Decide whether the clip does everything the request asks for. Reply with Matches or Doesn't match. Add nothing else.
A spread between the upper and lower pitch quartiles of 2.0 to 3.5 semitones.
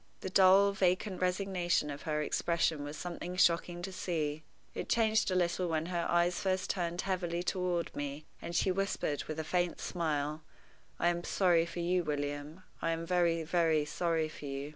Matches